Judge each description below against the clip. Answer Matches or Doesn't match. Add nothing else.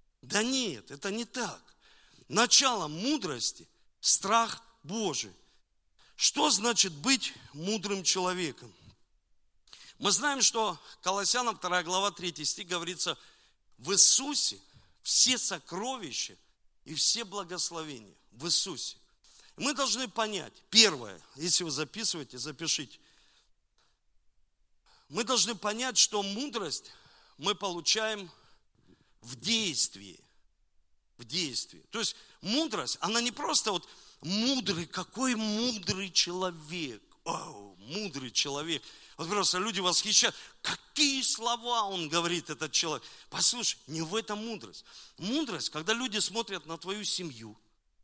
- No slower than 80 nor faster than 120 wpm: Matches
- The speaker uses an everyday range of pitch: Doesn't match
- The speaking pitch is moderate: Doesn't match